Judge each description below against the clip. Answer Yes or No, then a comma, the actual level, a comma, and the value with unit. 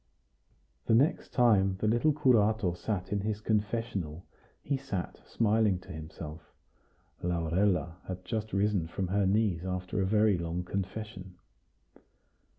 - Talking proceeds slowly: Yes, slow, 130 wpm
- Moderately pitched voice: No, low, 100 Hz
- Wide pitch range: No, average, 3.4 semitones